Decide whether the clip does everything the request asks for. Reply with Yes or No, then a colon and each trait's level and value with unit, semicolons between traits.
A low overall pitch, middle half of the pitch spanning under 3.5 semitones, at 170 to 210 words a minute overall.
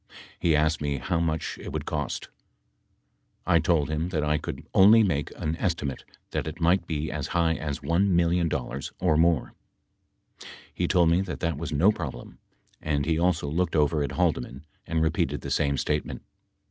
Yes: very low, 80 Hz; narrow, 2.5 semitones; average, 175 wpm